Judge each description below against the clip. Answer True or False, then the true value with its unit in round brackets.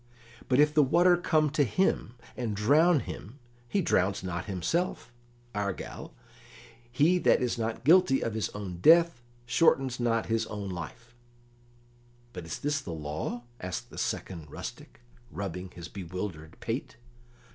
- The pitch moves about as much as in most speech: False (7.9 semitones)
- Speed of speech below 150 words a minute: True (140 wpm)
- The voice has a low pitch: True (115 Hz)